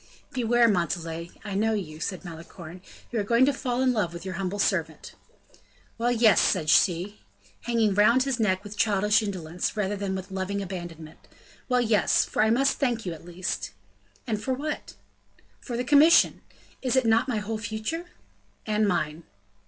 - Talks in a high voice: Yes, high, 210 Hz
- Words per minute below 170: No, average, 175 wpm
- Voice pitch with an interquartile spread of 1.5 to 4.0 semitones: No, average, 4.5 semitones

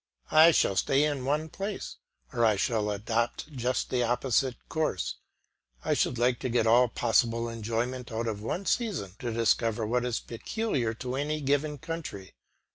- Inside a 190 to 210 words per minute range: No, average, 165 wpm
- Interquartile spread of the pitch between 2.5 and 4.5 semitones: Yes, average, 3.9 semitones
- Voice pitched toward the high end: No, low, 120 Hz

